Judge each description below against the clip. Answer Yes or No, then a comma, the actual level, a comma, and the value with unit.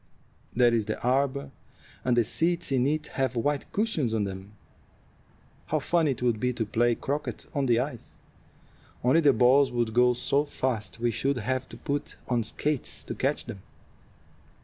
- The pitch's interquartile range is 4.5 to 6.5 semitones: No, average, 3.3 semitones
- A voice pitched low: Yes, low, 125 Hz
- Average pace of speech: Yes, average, 170 wpm